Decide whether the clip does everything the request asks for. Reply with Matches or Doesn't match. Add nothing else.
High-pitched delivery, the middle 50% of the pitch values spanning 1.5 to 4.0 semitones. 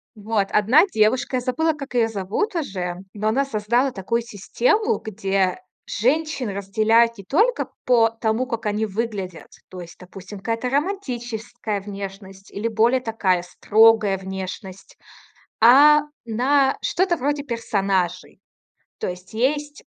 Doesn't match